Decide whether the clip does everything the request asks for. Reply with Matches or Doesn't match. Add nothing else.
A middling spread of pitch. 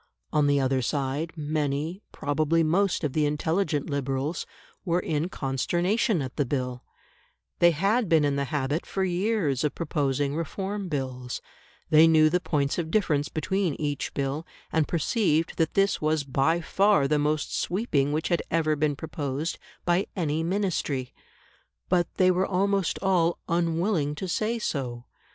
Matches